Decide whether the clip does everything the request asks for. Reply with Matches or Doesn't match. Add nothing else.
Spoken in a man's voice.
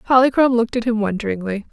Doesn't match